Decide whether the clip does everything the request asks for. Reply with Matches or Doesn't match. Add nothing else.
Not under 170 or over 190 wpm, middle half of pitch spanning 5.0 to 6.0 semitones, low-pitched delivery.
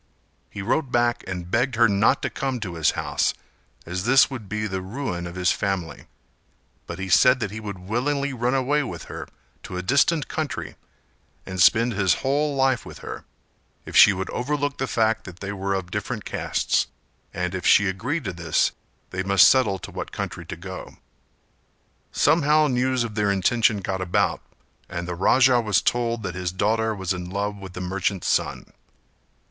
Matches